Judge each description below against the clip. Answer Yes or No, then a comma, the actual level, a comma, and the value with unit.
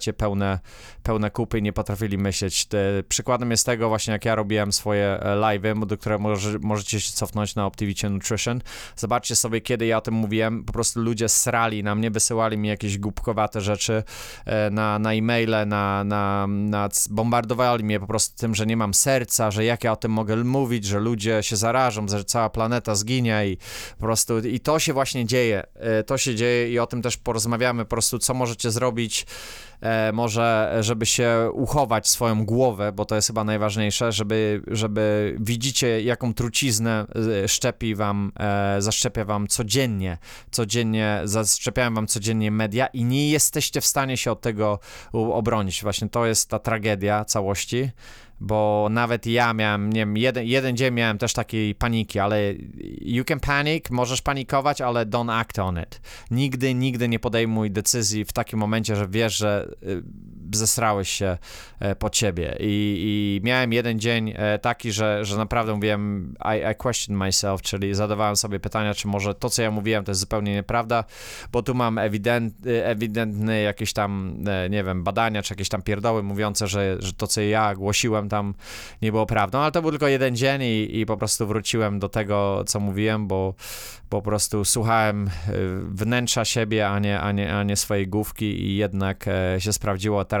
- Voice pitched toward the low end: Yes, low, 110 Hz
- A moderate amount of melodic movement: No, narrow, 2.2 semitones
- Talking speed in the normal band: No, fast, 175 wpm